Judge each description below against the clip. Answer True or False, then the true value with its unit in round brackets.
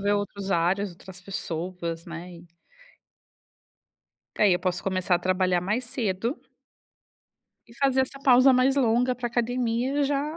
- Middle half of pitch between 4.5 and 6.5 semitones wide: True (5.6 semitones)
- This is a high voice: True (205 Hz)